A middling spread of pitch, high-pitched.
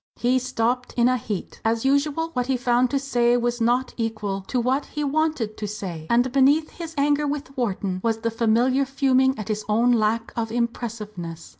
Yes: average, 3.2 semitones; high, 240 Hz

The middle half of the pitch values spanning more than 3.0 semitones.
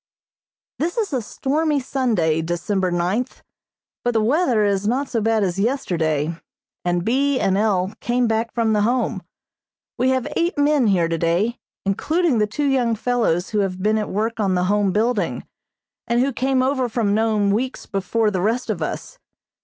Yes: average, 4.7 semitones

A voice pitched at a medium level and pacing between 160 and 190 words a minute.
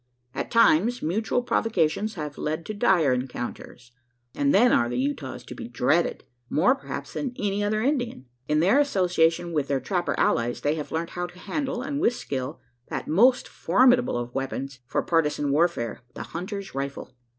Yes: medium, 170 Hz; average, 175 wpm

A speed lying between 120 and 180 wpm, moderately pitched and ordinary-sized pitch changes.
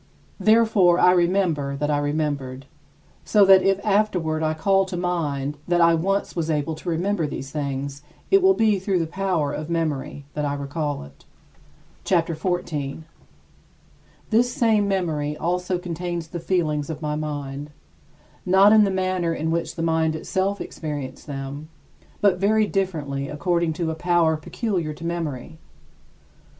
Yes: average, 155 wpm; medium, 165 Hz; average, 4.0 semitones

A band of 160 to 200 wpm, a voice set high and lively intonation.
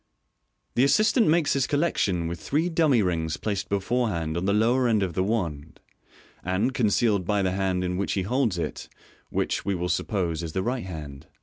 No: average, 190 wpm; very low, 95 Hz; wide, 5.8 semitones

